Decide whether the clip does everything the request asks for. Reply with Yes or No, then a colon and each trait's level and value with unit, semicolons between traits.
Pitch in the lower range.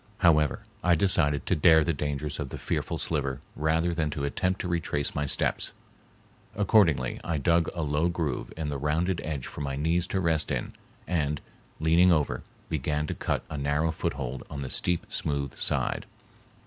Yes: very low, 75 Hz